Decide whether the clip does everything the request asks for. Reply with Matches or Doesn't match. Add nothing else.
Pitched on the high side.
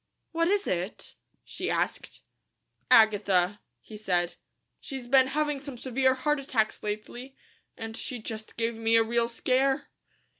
Matches